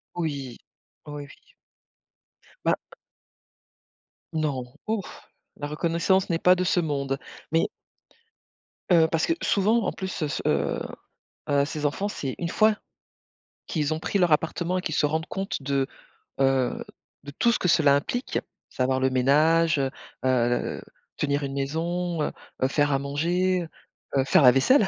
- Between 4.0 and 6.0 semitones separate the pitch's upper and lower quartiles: Yes, average, 4.3 semitones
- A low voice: No, medium, 155 Hz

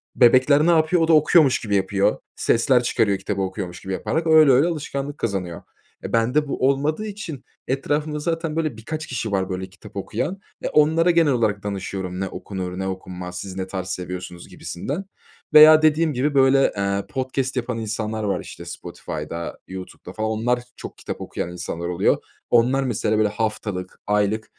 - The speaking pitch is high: No, low, 115 Hz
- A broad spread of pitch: Yes, wide, 7.4 semitones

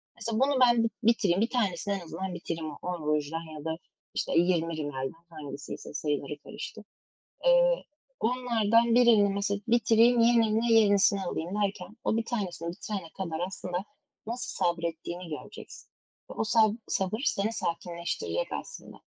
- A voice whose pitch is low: No, high, 195 Hz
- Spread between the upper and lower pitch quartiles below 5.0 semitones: No, wide, 5.5 semitones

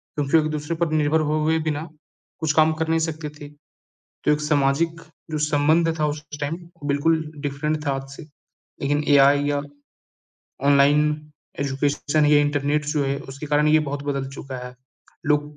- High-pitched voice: No, medium, 150 Hz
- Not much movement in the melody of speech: Yes, narrow, 1.5 semitones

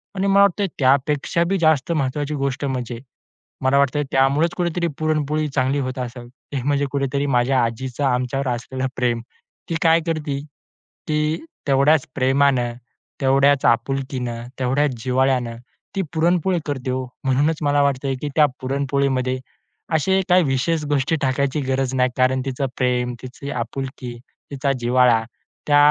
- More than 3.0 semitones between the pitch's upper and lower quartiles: No, narrow, 2.5 semitones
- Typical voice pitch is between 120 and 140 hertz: Yes, low, 135 Hz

